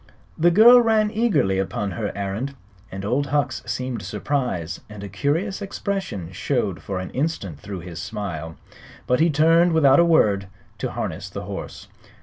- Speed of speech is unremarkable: Yes, average, 155 wpm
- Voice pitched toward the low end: Yes, low, 130 Hz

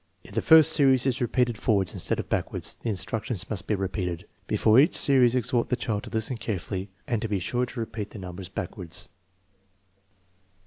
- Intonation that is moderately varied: Yes, average, 4.2 semitones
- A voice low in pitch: Yes, low, 110 Hz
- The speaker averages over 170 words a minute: Yes, average, 190 wpm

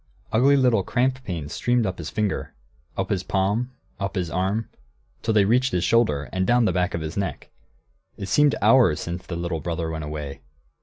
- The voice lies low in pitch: Yes, very low, 95 Hz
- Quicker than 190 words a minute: Yes, average, 200 wpm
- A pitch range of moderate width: No, wide, 5.7 semitones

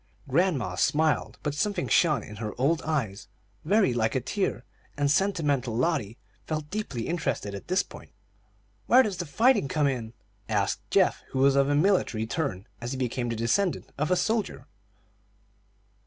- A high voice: No, medium, 140 Hz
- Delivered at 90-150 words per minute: No, average, 160 wpm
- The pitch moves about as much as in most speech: No, wide, 6.7 semitones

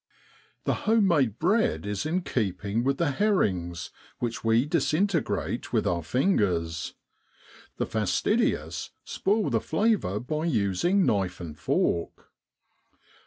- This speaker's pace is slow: Yes, slow, 120 wpm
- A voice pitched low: Yes, low, 125 Hz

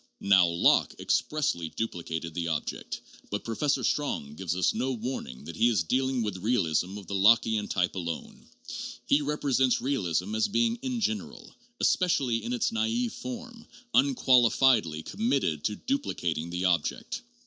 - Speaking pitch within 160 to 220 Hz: No, low, 115 Hz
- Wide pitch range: Yes, wide, 9.0 semitones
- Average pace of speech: Yes, average, 145 wpm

